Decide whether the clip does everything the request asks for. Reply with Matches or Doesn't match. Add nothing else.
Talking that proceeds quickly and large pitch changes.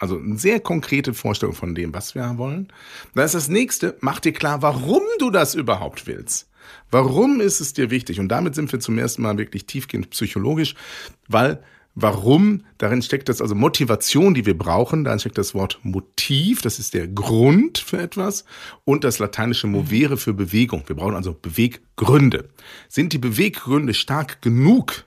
Doesn't match